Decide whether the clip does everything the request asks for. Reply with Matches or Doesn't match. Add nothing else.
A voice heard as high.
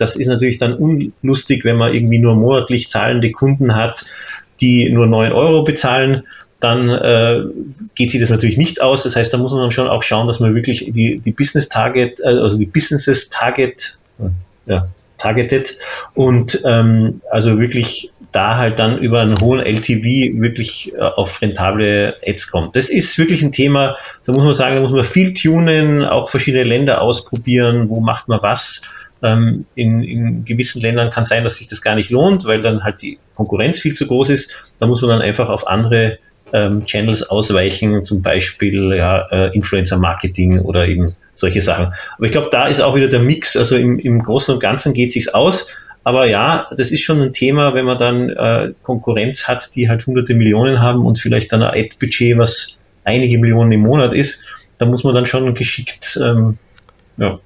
Doesn't match